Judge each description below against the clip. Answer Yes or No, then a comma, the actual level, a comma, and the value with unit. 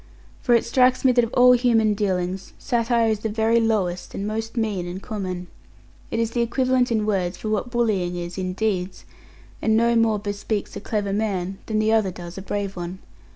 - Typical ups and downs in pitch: Yes, average, 3.3 semitones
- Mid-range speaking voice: No, high, 215 Hz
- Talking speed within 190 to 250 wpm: Yes, average, 200 wpm